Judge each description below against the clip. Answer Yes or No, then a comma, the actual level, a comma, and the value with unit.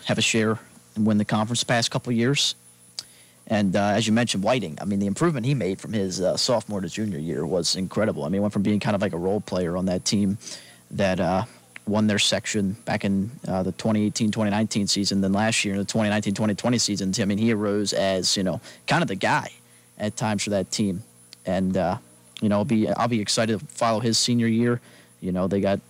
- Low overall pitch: Yes, low, 105 Hz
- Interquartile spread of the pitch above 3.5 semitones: No, average, 2.8 semitones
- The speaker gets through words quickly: Yes, fast, 230 wpm